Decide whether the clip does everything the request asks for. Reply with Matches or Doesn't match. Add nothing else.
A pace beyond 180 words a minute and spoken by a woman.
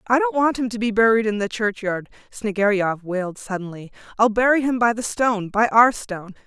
Matches